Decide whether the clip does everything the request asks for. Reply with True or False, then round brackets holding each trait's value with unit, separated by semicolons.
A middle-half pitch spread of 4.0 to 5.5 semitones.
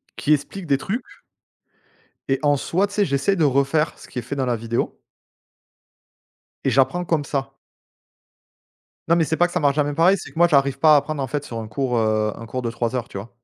True (4.3 semitones)